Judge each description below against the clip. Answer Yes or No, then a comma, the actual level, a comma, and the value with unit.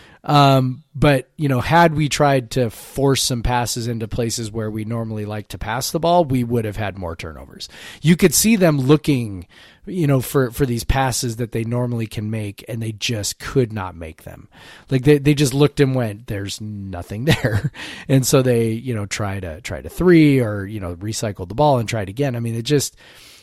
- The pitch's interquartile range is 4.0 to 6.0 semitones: Yes, average, 4.7 semitones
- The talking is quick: Yes, fast, 215 wpm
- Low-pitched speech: Yes, low, 120 Hz